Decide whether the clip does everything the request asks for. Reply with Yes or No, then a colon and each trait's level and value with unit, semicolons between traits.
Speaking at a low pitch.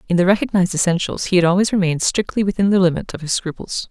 No: medium, 180 Hz